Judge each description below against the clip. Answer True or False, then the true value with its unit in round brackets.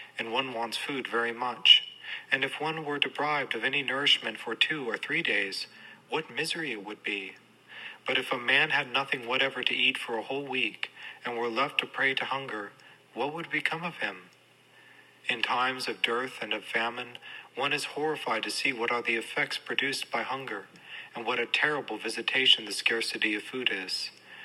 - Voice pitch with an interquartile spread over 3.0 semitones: False (2.4 semitones)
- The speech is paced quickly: False (190 wpm)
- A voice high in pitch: False (120 Hz)